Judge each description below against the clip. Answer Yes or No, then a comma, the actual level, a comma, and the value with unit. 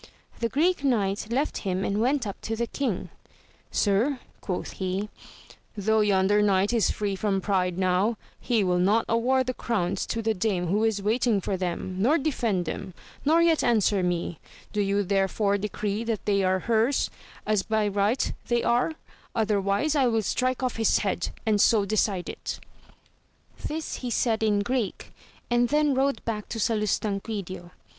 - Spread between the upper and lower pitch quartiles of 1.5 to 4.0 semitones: Yes, average, 3.3 semitones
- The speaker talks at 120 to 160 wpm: No, average, 180 wpm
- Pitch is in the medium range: No, high, 215 Hz